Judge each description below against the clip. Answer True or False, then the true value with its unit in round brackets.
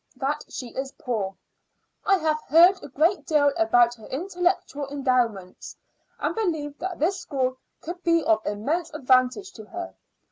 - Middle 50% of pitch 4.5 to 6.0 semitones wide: True (5.2 semitones)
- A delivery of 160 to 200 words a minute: False (150 wpm)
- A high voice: True (290 Hz)